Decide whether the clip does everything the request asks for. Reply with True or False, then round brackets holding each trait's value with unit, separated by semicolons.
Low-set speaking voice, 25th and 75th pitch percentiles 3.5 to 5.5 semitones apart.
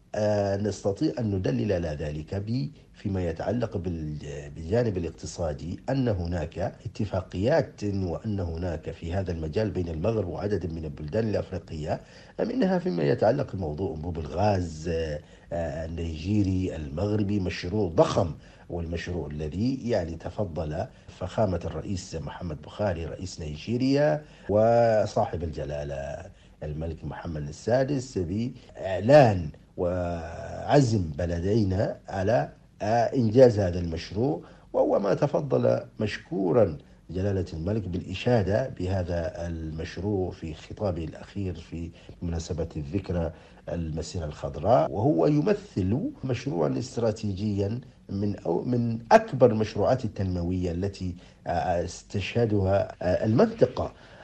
True (95 Hz; 4.4 semitones)